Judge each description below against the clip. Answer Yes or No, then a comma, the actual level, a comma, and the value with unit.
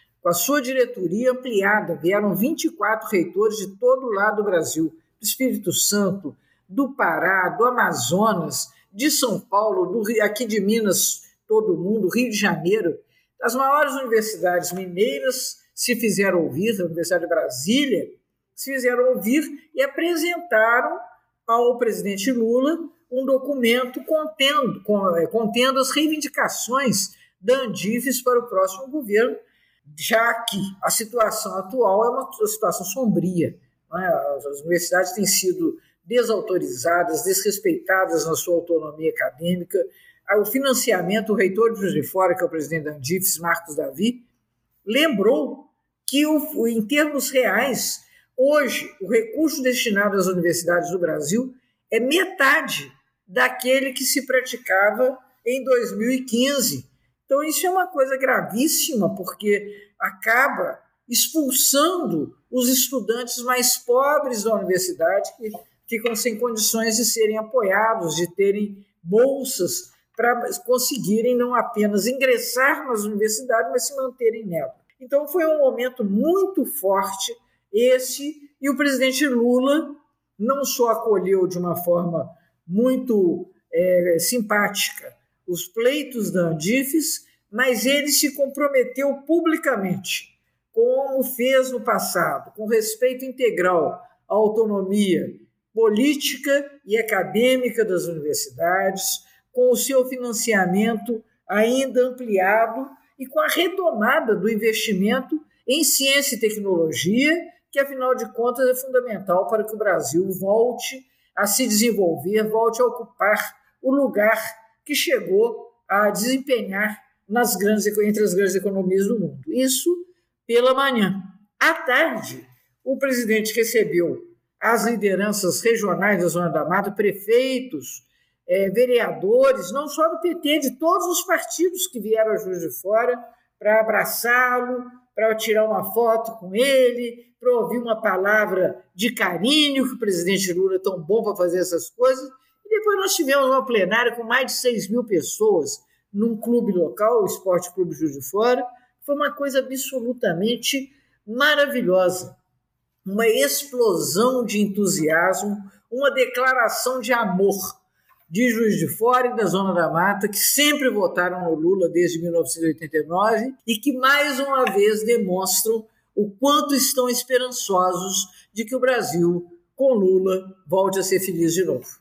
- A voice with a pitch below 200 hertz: No, high, 230 Hz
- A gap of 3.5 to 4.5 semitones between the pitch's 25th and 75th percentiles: No, average, 5.3 semitones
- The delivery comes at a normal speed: Yes, average, 130 wpm